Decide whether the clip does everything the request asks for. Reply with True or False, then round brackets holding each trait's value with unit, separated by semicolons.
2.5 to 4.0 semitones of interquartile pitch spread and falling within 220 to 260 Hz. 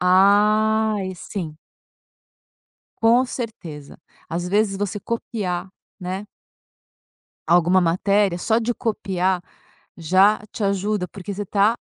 False (2.9 semitones; 195 Hz)